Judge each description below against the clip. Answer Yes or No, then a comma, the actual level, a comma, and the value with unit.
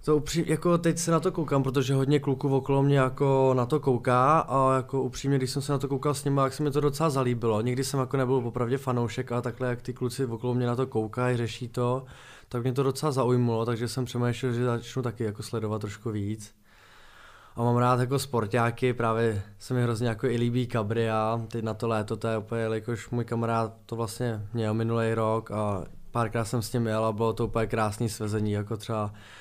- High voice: No, low, 120 Hz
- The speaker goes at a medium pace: No, fast, 220 wpm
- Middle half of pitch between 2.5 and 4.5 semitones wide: Yes, average, 2.8 semitones